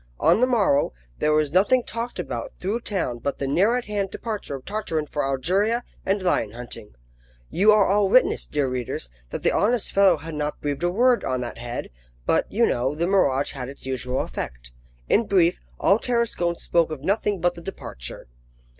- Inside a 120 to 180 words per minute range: No, average, 190 wpm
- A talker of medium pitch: Yes, medium, 175 Hz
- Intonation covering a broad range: Yes, wide, 7.2 semitones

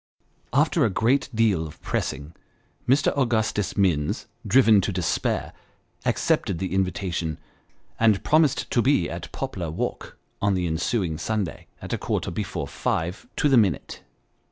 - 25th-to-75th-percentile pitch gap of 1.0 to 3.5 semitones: No, wide, 5.5 semitones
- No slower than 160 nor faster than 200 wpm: No, average, 140 wpm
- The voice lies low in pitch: Yes, low, 100 Hz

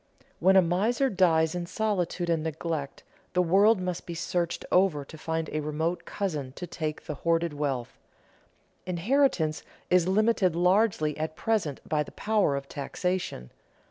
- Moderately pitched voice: Yes, medium, 170 Hz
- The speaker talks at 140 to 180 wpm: Yes, average, 150 wpm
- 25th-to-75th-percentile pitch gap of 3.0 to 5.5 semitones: Yes, average, 3.5 semitones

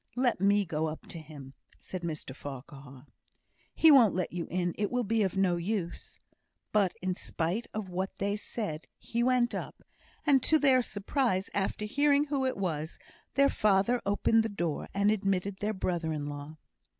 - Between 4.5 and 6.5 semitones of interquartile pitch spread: Yes, average, 5.2 semitones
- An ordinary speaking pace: Yes, average, 175 wpm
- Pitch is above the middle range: Yes, high, 195 Hz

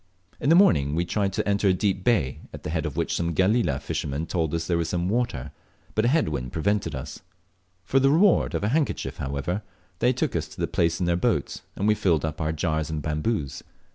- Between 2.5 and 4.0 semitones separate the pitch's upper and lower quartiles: No, wide, 5.6 semitones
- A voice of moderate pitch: No, very low, 85 Hz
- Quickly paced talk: Yes, fast, 230 wpm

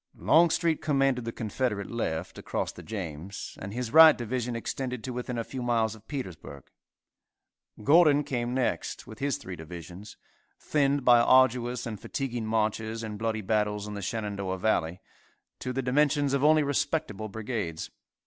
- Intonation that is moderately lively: Yes, average, 4.1 semitones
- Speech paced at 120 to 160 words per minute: Yes, average, 155 wpm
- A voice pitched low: Yes, low, 115 Hz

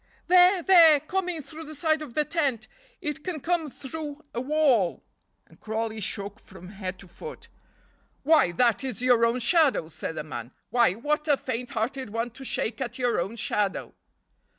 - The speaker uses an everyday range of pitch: No, wide, 6.0 semitones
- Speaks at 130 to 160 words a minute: No, average, 175 wpm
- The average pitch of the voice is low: No, very high, 255 Hz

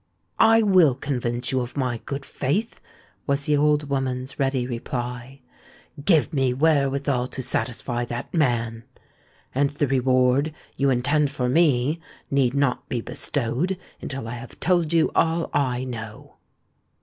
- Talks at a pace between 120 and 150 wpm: Yes, average, 140 wpm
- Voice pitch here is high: No, low, 135 Hz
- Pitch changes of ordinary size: Yes, average, 3.0 semitones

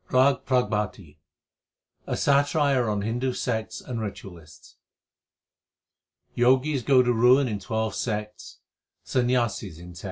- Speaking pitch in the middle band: No, low, 115 Hz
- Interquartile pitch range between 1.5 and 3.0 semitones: No, average, 3.6 semitones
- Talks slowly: Yes, slow, 115 wpm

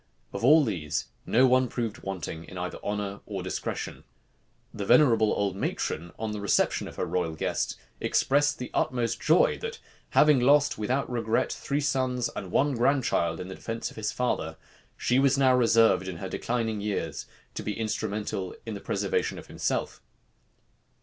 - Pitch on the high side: No, low, 115 Hz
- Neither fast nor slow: Yes, average, 165 wpm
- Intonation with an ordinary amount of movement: Yes, average, 4.8 semitones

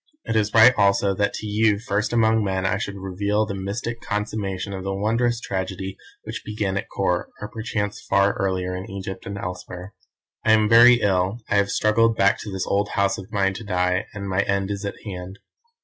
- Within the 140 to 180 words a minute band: No, fast, 205 wpm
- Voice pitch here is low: Yes, low, 100 Hz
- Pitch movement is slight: Yes, narrow, 2.0 semitones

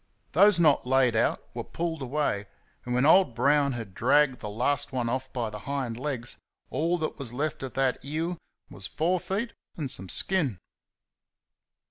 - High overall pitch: No, low, 135 Hz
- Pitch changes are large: No, average, 4.3 semitones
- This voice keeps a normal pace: Yes, average, 170 wpm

